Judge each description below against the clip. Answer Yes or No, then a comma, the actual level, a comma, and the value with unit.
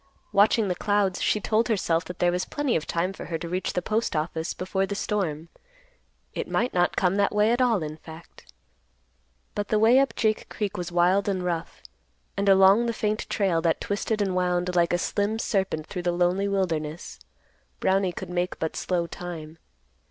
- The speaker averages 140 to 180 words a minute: No, average, 190 wpm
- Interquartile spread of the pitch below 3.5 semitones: Yes, average, 3.0 semitones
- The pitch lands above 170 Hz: Yes, medium, 185 Hz